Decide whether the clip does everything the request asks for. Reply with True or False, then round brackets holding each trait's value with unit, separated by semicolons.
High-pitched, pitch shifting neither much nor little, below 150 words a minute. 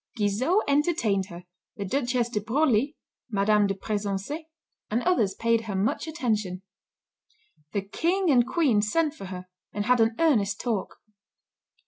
False (225 Hz; 6.1 semitones; 140 wpm)